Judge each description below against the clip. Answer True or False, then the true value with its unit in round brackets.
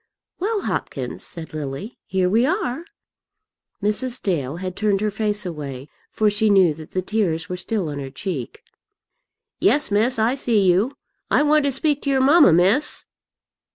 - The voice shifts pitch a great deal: True (6.6 semitones)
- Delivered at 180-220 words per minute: False (165 wpm)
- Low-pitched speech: False (205 Hz)